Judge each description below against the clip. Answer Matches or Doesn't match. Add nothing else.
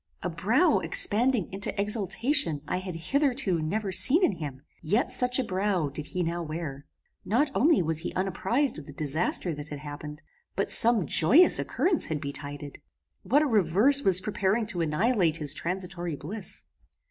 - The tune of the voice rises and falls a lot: Matches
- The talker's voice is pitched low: Doesn't match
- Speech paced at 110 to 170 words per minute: Matches